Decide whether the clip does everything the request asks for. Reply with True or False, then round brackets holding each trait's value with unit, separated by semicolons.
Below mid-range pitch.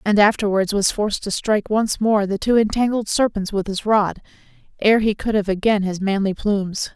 False (205 Hz)